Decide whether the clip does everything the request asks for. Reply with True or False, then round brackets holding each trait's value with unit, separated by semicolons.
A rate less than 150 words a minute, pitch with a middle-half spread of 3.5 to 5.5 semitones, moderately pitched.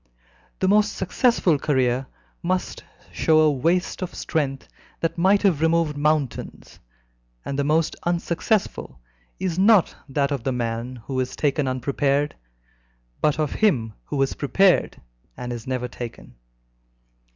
True (135 wpm; 4.8 semitones; 150 Hz)